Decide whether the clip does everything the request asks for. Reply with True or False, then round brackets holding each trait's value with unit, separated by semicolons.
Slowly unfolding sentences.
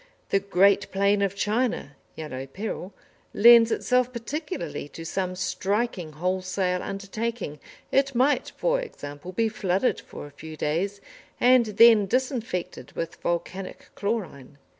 True (125 wpm)